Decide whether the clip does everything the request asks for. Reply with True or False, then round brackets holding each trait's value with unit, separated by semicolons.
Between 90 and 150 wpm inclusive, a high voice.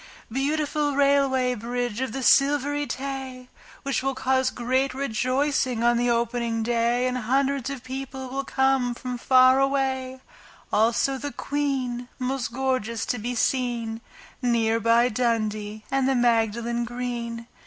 True (135 wpm; 255 Hz)